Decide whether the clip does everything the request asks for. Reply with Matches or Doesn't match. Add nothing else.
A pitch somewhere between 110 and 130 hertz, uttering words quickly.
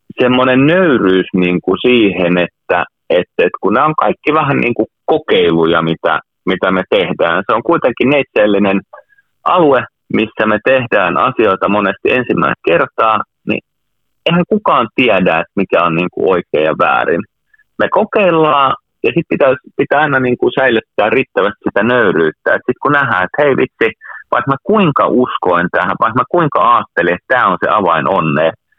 Matches